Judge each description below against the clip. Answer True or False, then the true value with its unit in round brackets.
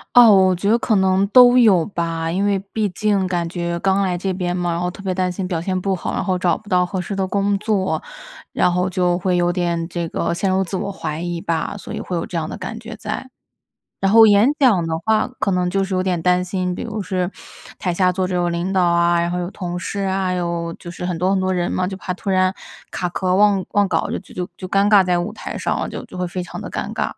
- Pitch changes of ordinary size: False (2.0 semitones)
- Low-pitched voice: False (185 Hz)